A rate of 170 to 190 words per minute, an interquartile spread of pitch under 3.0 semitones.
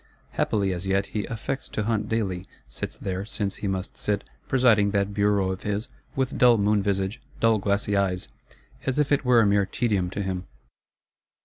Yes: average, 185 wpm; narrow, 2.4 semitones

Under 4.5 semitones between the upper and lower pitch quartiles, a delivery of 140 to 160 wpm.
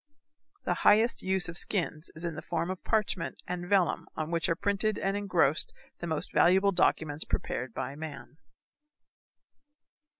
Yes: average, 3.7 semitones; average, 155 wpm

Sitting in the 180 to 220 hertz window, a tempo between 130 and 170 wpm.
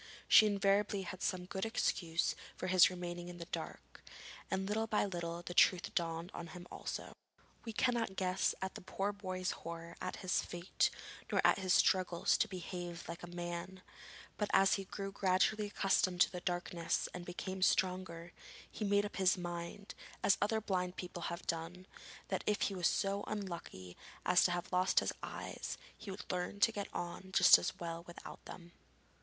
No: medium, 185 Hz; average, 180 wpm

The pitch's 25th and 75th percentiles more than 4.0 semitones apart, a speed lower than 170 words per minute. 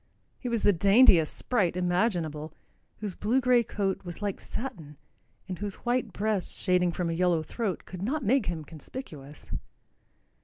Yes: average, 5.1 semitones; average, 155 wpm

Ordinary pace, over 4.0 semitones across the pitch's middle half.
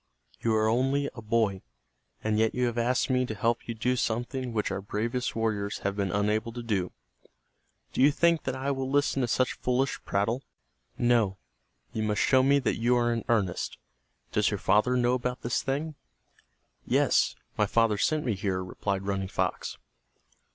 No: average, 180 wpm; average, 3.3 semitones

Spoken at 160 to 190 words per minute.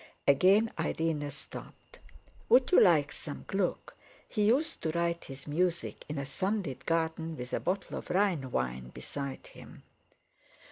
No: average, 145 wpm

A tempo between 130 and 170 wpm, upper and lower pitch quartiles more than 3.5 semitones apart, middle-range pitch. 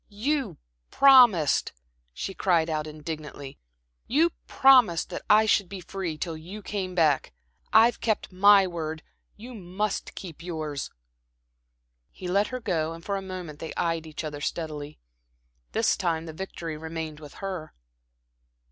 Yes: average, 145 wpm; average, 4.4 semitones; medium, 175 Hz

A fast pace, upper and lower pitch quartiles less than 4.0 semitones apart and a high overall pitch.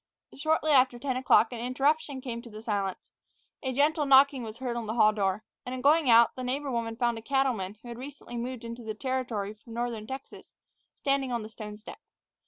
Yes: fast, 210 wpm; average, 3.0 semitones; high, 245 Hz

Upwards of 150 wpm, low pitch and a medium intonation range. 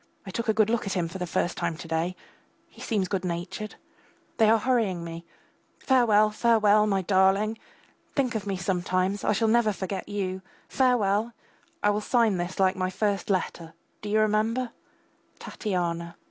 No: average, 175 wpm; high, 205 Hz; average, 3.0 semitones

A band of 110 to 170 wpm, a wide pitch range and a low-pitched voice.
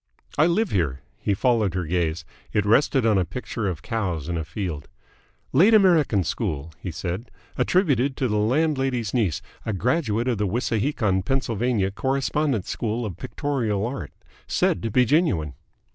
Yes: average, 160 wpm; wide, 6.3 semitones; low, 110 Hz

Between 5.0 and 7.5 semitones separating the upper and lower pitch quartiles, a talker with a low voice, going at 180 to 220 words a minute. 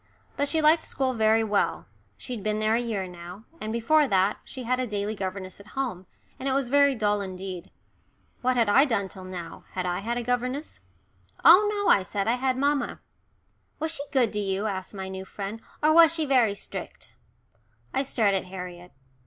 No: wide, 5.5 semitones; high, 220 Hz; average, 200 wpm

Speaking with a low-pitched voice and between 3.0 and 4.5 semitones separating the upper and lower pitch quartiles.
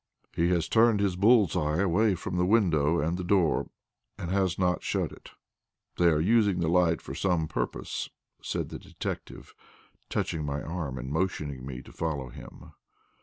Yes: very low, 85 Hz; average, 3.7 semitones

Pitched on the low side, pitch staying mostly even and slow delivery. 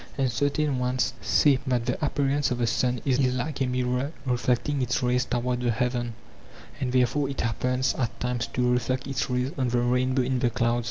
No: low, 125 Hz; narrow, 1.3 semitones; average, 200 wpm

